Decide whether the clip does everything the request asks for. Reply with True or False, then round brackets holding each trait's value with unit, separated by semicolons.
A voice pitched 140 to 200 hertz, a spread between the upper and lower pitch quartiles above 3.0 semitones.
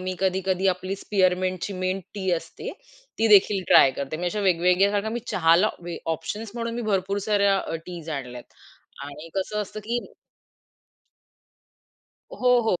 False (190 Hz; 2.7 semitones)